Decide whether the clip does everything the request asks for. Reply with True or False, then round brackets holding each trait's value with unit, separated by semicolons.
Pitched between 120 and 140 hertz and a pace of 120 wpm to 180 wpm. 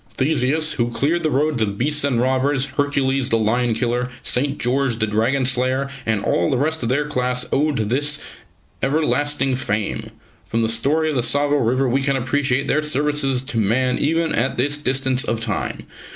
False (135 Hz; 190 wpm)